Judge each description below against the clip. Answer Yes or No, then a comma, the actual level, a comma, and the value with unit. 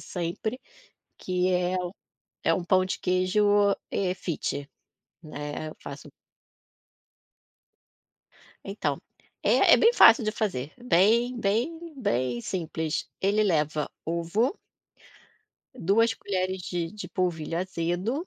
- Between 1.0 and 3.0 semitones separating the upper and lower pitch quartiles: No, average, 4.3 semitones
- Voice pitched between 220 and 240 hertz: No, medium, 185 Hz